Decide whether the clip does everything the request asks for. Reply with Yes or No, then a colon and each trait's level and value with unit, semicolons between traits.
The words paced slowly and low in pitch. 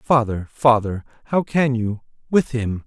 Yes: slow, 125 wpm; low, 120 Hz